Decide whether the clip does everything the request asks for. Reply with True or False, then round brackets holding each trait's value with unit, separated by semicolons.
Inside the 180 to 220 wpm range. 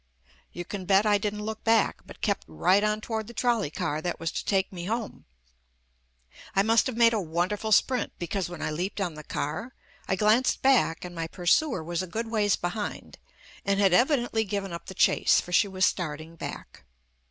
True (200 wpm)